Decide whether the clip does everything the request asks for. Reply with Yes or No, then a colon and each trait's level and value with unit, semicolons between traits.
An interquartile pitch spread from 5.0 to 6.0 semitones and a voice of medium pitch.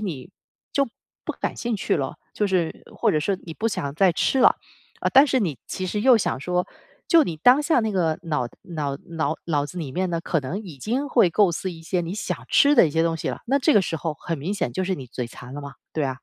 Yes: wide, 5.6 semitones; medium, 175 Hz